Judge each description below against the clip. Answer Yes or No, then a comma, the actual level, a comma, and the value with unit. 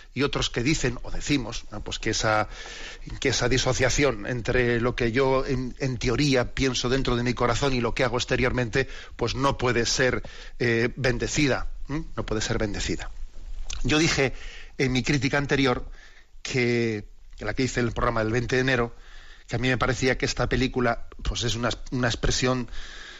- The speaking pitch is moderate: No, low, 125 Hz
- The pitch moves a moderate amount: No, narrow, 2.2 semitones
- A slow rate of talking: No, average, 185 wpm